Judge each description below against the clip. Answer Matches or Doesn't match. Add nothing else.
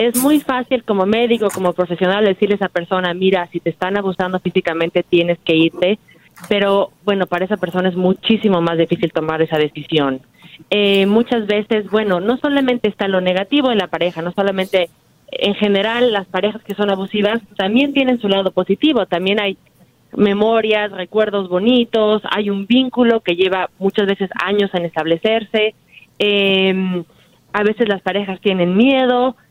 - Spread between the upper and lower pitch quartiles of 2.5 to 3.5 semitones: Matches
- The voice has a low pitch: Doesn't match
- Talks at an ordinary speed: Matches